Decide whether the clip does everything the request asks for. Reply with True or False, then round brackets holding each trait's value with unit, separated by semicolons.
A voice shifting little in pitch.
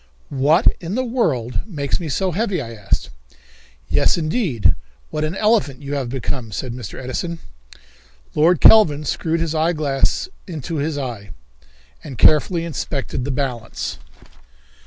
False (4.5 semitones)